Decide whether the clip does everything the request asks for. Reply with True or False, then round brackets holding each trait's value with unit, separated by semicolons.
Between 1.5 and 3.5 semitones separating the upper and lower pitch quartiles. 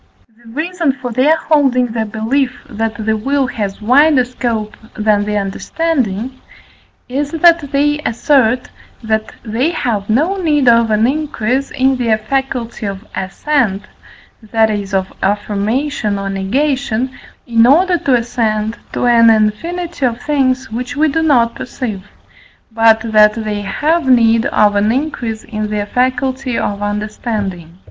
False (4.3 semitones)